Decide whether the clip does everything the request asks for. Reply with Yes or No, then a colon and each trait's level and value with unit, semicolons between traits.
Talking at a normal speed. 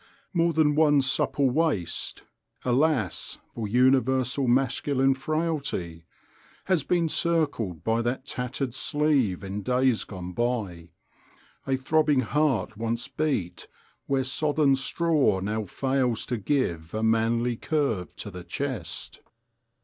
No: slow, 120 wpm